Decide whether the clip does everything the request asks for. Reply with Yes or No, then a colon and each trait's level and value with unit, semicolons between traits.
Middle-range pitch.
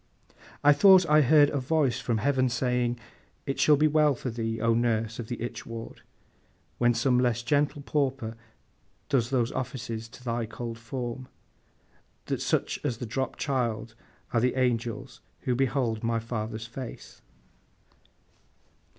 No: low, 120 Hz